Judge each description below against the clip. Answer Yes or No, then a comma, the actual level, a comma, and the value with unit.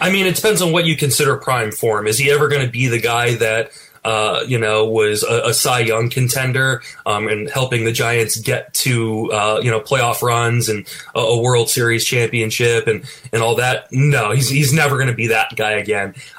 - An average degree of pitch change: Yes, average, 3.2 semitones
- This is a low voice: Yes, low, 120 Hz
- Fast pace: Yes, fast, 220 wpm